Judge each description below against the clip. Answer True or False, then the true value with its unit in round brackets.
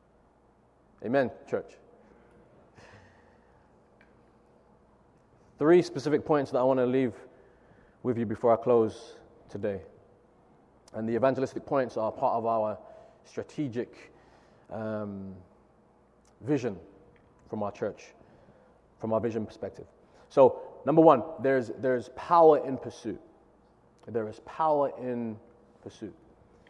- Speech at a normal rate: False (105 wpm)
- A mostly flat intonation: False (4.9 semitones)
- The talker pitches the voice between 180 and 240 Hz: False (125 Hz)